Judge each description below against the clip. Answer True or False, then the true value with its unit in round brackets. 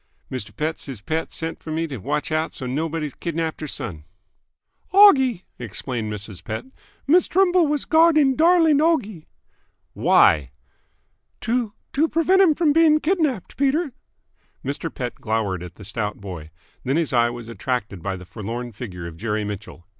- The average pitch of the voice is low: False (150 Hz)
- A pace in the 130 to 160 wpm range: True (155 wpm)